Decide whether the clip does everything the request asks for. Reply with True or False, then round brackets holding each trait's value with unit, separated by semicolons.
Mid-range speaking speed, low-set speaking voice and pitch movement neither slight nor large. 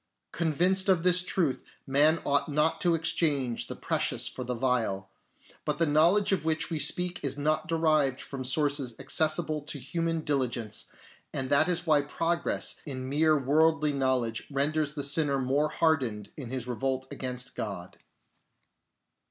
False (150 wpm; 145 Hz; 3.5 semitones)